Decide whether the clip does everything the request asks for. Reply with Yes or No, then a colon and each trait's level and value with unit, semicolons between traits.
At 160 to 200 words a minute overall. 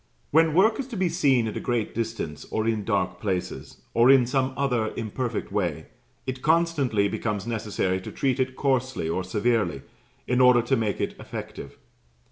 Yes: average, 175 wpm